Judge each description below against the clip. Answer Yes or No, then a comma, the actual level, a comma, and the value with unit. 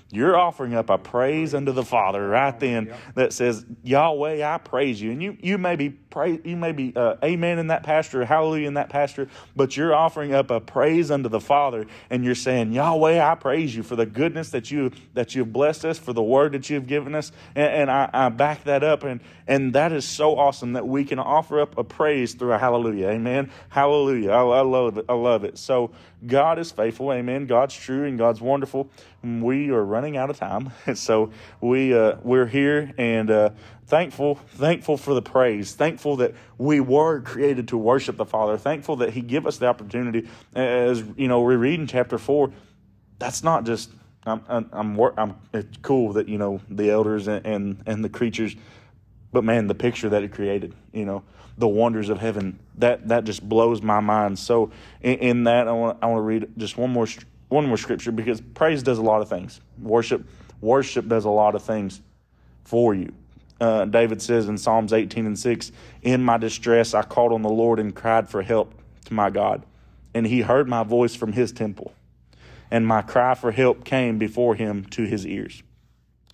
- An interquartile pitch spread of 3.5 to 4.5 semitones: Yes, average, 3.9 semitones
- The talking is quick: Yes, fast, 210 wpm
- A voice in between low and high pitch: No, low, 120 Hz